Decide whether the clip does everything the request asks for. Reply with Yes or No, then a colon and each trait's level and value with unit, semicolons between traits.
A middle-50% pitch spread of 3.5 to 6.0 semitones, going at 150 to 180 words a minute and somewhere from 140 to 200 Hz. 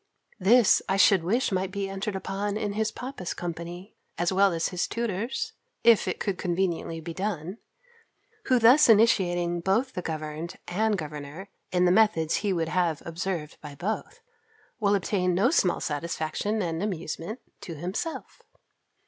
Yes: average, 3.8 semitones; average, 155 wpm; high, 190 Hz